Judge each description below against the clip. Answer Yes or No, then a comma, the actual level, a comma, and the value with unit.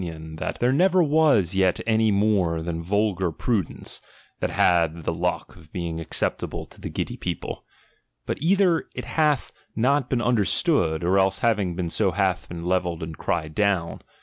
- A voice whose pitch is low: Yes, very low, 95 Hz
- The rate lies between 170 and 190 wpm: Yes, average, 175 wpm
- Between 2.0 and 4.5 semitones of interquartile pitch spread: No, average, 5.1 semitones